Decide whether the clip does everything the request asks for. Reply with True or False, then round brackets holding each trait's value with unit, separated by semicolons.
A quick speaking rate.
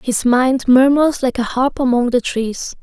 False (190 wpm)